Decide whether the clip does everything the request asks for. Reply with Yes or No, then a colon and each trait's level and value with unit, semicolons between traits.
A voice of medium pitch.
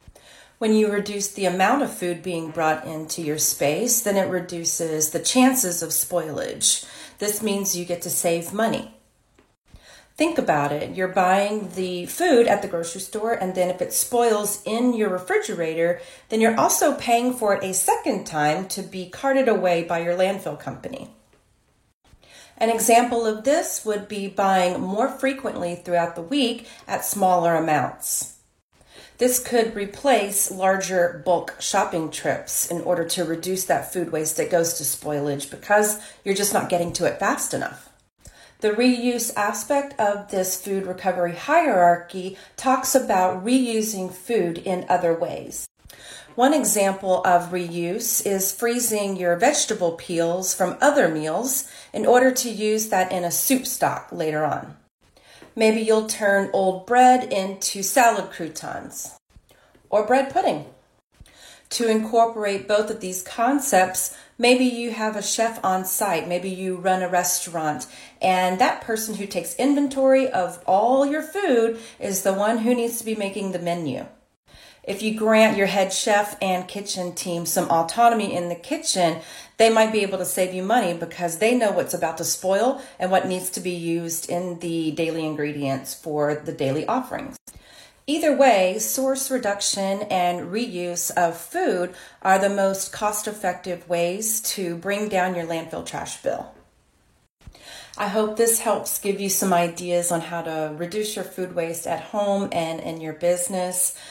No: high, 195 Hz